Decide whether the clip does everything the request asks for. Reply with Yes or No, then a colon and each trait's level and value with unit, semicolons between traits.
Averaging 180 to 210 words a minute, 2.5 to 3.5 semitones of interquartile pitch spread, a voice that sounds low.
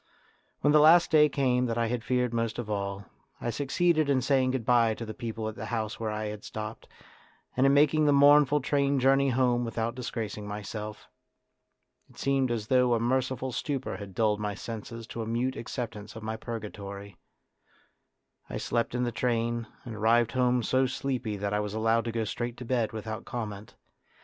Yes: average, 190 wpm; average, 3.1 semitones; low, 120 Hz